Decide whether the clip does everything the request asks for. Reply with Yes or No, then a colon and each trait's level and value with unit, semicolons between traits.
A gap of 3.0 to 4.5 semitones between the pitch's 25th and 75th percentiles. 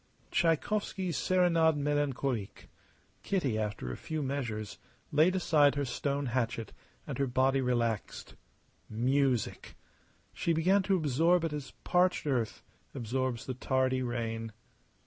No: average, 5.0 semitones